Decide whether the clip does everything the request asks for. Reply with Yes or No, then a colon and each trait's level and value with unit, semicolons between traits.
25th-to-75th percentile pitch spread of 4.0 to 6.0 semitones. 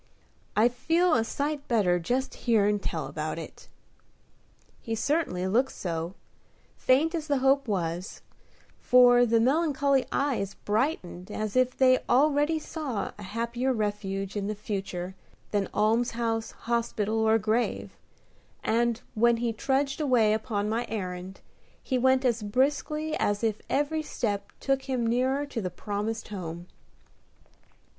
Yes: average, 4.4 semitones